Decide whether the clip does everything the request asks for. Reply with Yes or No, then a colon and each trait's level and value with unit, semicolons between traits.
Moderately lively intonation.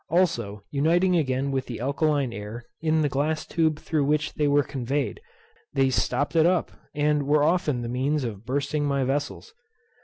Yes: average, 3.0 semitones